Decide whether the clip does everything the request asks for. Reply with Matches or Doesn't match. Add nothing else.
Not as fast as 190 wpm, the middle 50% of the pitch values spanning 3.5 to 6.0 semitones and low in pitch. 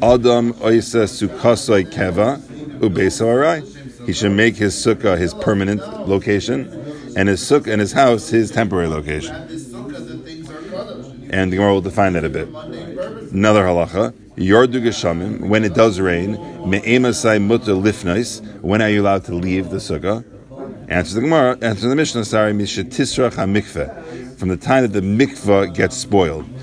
Matches